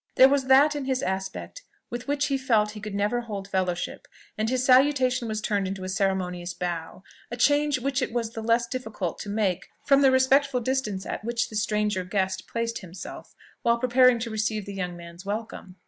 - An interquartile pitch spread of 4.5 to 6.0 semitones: Yes, average, 5.0 semitones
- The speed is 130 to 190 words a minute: No, fast, 205 wpm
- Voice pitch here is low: No, high, 220 Hz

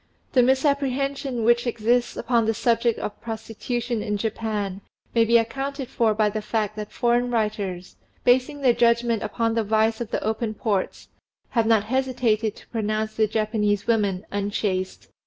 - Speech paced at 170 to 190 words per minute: No, average, 155 wpm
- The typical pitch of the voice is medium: No, high, 225 Hz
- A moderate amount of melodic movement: No, narrow, 2.2 semitones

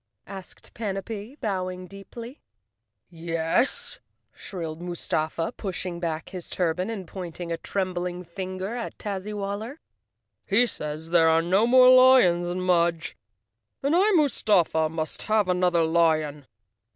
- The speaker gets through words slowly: Yes, slow, 125 wpm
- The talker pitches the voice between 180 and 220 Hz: Yes, medium, 185 Hz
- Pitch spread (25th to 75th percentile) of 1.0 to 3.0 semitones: No, average, 3.7 semitones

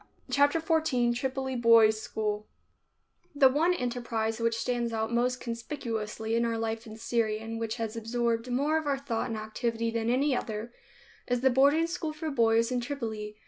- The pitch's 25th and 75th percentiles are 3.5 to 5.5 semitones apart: No, average, 2.9 semitones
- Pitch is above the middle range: Yes, high, 235 Hz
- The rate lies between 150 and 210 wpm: Yes, average, 175 wpm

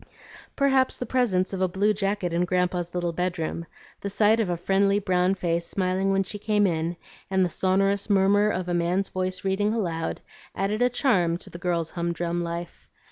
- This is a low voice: No, medium, 185 Hz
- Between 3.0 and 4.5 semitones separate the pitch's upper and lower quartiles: No, narrow, 2.6 semitones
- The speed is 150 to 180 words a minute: No, average, 190 wpm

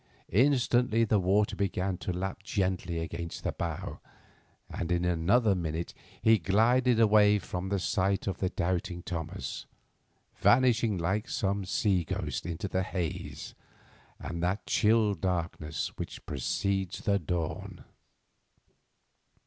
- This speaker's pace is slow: Yes, slow, 125 wpm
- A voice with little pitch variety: No, average, 3.2 semitones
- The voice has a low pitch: Yes, very low, 95 Hz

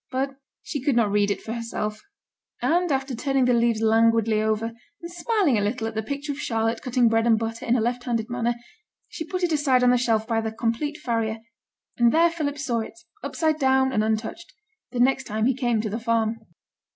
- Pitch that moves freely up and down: No, average, 3.3 semitones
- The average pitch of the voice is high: Yes, high, 235 Hz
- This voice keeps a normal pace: No, fast, 215 wpm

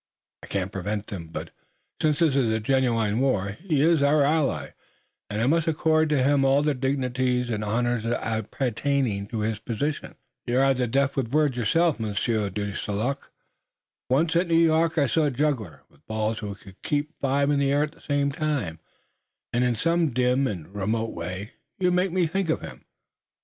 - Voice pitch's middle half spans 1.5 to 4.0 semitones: No, wide, 5.4 semitones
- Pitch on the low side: Yes, low, 130 Hz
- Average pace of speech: Yes, average, 185 wpm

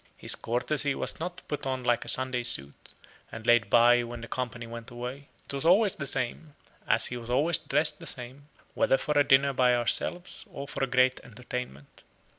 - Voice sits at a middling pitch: No, low, 130 Hz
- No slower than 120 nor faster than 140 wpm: No, average, 200 wpm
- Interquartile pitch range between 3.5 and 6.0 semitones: No, average, 2.8 semitones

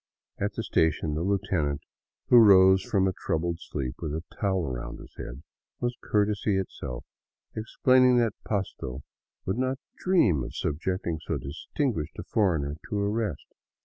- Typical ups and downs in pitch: No, wide, 5.8 semitones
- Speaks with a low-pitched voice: Yes, very low, 95 Hz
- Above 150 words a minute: No, average, 145 wpm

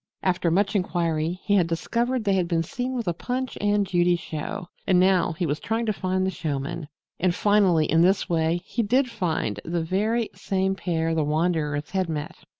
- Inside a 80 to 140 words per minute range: No, average, 195 wpm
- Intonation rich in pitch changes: No, average, 3.7 semitones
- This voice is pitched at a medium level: Yes, medium, 180 Hz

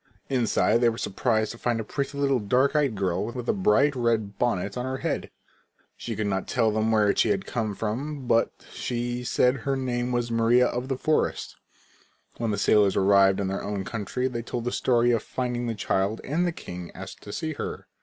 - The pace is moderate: No, fast, 210 wpm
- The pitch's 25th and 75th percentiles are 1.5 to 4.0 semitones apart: Yes, average, 3.3 semitones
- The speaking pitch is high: No, low, 120 Hz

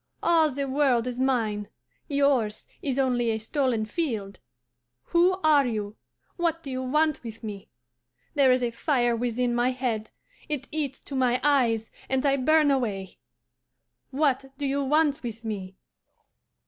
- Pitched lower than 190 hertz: No, very high, 255 Hz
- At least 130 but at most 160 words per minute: Yes, average, 150 wpm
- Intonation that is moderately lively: Yes, average, 3.7 semitones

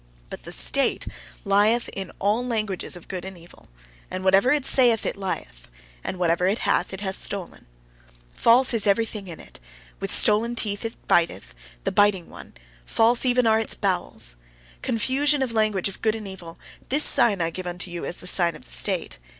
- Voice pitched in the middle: No, high, 200 Hz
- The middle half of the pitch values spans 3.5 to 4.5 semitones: Yes, average, 4.1 semitones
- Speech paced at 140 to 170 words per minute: No, average, 190 wpm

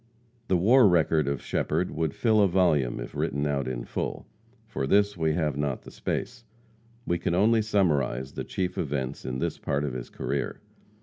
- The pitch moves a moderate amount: No, wide, 5.8 semitones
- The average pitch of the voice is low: Yes, very low, 80 Hz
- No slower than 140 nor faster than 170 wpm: No, average, 185 wpm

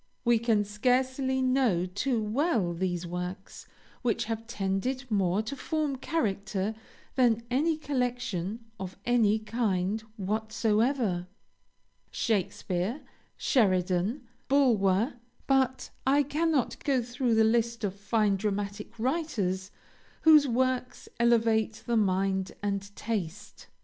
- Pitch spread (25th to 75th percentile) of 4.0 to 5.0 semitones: Yes, average, 4.6 semitones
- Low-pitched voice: No, high, 225 Hz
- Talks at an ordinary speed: No, slow, 110 wpm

